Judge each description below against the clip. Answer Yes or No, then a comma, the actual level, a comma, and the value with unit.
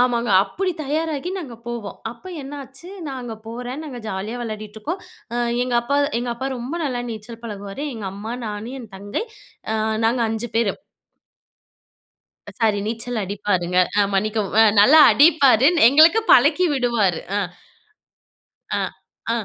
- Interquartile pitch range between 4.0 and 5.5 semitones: Yes, average, 4.3 semitones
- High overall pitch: Yes, high, 235 Hz